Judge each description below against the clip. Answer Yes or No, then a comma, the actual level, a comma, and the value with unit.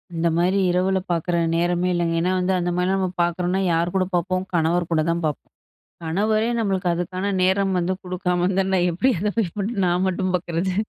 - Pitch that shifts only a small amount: Yes, narrow, 1.6 semitones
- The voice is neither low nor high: Yes, medium, 180 Hz